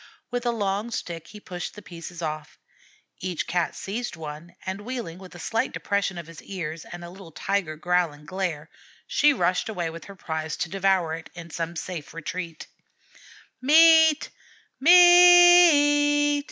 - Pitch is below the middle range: No, medium, 185 Hz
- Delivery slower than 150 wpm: No, average, 165 wpm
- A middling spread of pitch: No, wide, 6.3 semitones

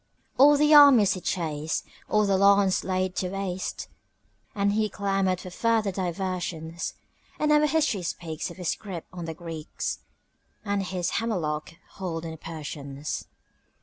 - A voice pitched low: No, medium, 185 Hz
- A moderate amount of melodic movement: Yes, average, 3.5 semitones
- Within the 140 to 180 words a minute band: Yes, average, 150 wpm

